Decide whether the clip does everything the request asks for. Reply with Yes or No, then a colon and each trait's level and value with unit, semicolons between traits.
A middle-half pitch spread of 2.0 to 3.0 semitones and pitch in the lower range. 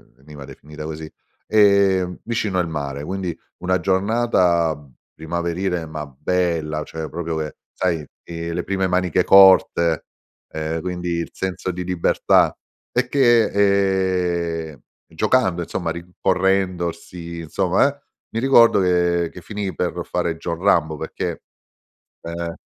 Yes: narrow, 2.5 semitones; very low, 90 Hz